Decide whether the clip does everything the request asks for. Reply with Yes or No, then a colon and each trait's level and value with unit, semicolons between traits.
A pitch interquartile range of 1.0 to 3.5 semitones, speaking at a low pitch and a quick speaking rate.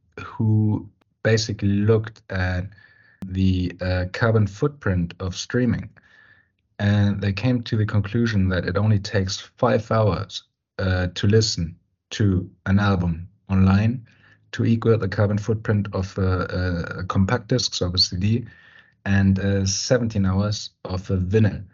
No: average, 2.9 semitones; low, 100 Hz; average, 140 wpm